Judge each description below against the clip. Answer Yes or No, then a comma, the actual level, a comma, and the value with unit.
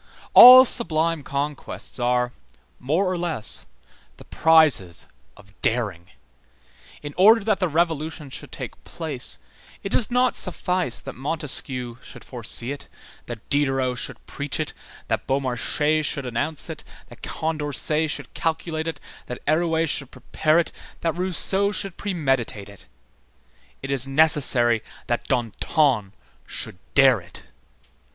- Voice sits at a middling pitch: Yes, medium, 145 Hz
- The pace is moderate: No, slow, 130 wpm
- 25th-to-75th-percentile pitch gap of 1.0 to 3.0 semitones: No, average, 4.8 semitones